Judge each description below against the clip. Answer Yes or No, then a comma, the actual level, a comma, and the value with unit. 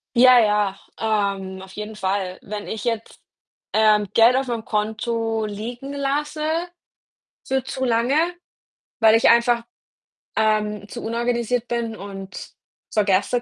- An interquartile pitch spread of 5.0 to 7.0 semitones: No, narrow, 2.5 semitones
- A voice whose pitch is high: Yes, high, 225 Hz